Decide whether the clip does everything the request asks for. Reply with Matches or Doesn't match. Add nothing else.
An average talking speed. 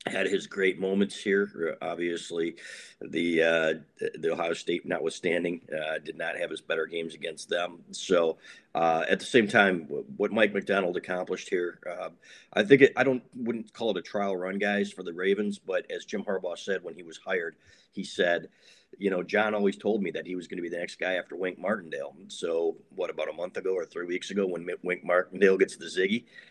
Doesn't match